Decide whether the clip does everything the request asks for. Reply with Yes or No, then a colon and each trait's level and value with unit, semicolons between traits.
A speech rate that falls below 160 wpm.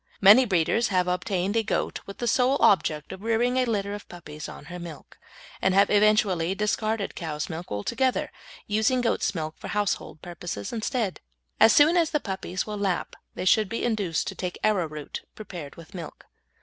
No: average, 180 wpm